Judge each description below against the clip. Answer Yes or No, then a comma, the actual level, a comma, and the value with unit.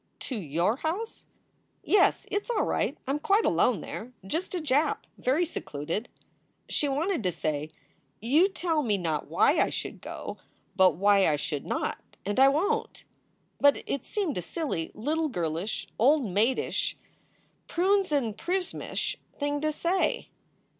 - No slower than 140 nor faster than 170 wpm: Yes, average, 155 wpm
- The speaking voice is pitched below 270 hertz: No, very high, 275 Hz